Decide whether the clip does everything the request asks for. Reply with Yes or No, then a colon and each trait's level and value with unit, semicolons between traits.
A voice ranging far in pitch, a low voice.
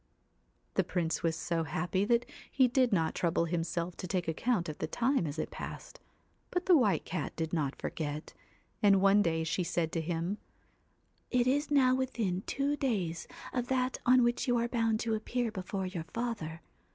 No: wide, 6.7 semitones; high, 195 Hz